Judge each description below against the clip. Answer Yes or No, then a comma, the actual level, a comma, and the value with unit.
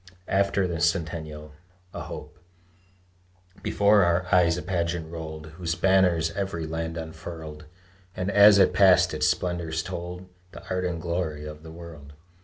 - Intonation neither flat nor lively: No, narrow, 2.3 semitones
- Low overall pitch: Yes, very low, 85 Hz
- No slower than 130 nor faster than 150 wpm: Yes, average, 145 wpm